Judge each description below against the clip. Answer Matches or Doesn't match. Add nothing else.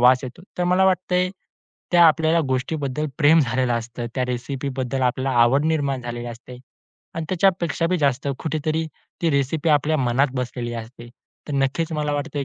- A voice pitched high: Doesn't match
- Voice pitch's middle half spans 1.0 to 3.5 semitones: Doesn't match